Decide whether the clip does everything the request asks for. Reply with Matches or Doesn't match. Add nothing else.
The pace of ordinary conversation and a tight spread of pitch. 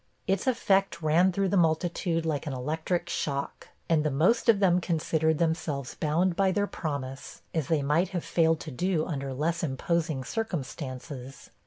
Doesn't match